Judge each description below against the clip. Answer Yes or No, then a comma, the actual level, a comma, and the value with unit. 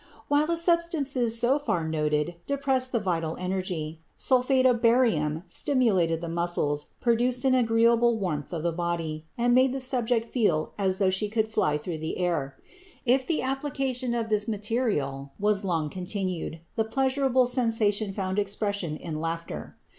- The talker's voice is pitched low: No, high, 210 Hz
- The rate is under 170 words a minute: Yes, average, 155 wpm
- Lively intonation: Yes, wide, 6.9 semitones